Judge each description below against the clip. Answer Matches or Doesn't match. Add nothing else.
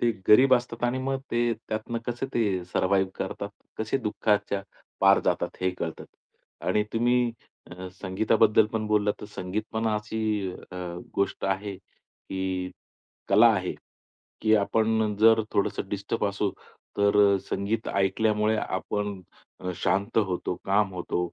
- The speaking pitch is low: Matches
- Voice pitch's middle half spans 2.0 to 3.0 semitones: Matches